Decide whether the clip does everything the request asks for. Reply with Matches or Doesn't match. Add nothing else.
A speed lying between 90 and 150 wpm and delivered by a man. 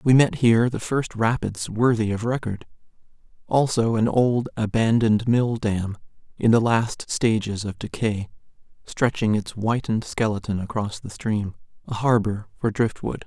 Matches